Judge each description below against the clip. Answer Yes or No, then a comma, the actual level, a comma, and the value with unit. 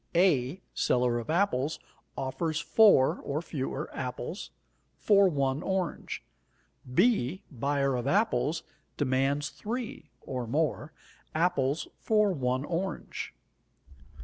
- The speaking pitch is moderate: Yes, medium, 150 Hz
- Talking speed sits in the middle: No, slow, 100 wpm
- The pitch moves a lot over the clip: Yes, wide, 5.7 semitones